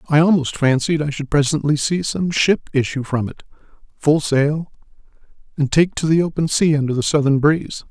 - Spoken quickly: No, average, 180 wpm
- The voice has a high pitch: No, medium, 150 Hz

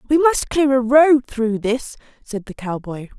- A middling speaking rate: Yes, average, 190 wpm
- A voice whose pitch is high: Yes, very high, 250 Hz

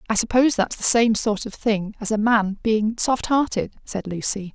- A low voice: No, high, 220 Hz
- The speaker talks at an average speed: No, fast, 210 wpm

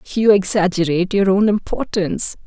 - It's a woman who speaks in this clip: Yes, female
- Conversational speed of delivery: No, slow, 120 wpm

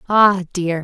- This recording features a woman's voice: Yes, female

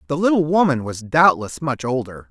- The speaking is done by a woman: No, male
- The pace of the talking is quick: Yes, fast, 210 wpm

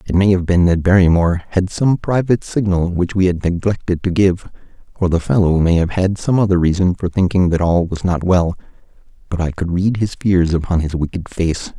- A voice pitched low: Yes, very low, 90 Hz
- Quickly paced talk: Yes, fast, 215 wpm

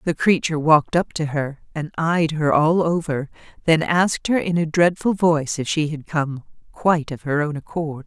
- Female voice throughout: Yes, female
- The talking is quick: No, average, 195 wpm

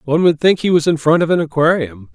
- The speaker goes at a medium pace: No, fast, 280 wpm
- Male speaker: Yes, male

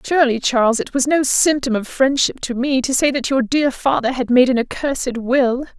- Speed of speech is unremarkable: No, fast, 220 wpm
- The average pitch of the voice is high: Yes, very high, 260 Hz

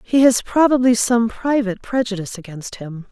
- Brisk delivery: No, average, 155 wpm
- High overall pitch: Yes, high, 225 Hz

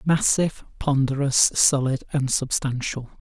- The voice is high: No, medium, 140 Hz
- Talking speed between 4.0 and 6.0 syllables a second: Yes, 4.3 syllables/s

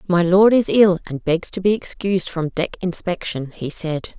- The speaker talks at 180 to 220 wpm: Yes, average, 200 wpm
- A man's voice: No, female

